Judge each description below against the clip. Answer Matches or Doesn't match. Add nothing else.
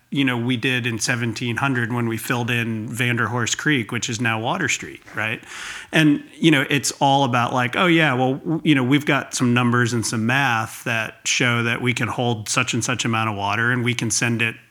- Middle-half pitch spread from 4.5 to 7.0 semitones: Doesn't match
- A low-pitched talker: Matches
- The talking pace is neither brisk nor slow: Doesn't match